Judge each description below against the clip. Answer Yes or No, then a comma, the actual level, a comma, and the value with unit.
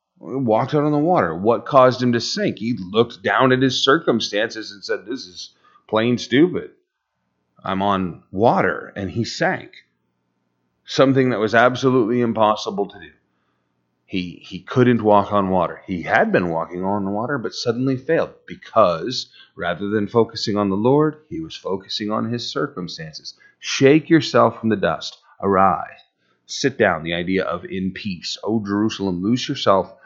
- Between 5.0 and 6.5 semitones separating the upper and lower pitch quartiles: Yes, wide, 5.5 semitones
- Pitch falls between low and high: No, low, 105 Hz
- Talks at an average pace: Yes, average, 160 wpm